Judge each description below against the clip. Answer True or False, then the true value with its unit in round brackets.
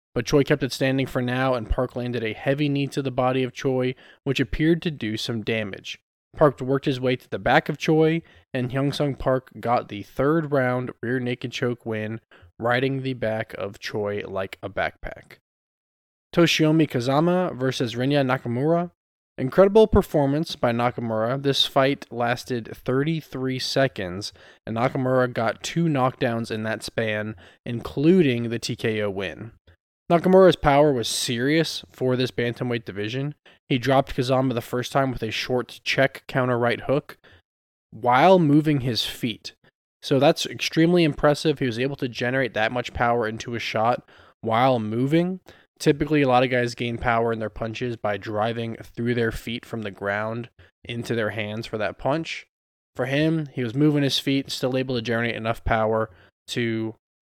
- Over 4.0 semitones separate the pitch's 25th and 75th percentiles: False (3.5 semitones)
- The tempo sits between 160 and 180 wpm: True (165 wpm)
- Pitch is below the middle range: True (125 Hz)